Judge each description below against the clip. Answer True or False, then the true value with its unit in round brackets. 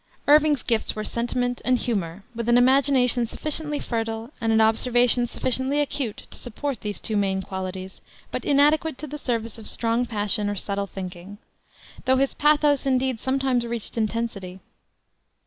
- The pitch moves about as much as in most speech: True (3.9 semitones)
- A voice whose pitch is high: True (240 Hz)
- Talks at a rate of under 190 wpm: True (155 wpm)